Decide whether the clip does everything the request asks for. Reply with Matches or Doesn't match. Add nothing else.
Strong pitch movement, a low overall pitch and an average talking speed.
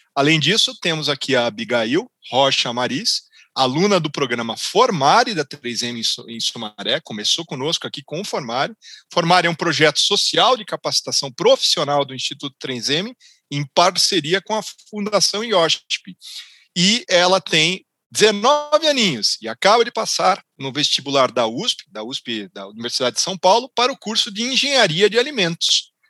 Doesn't match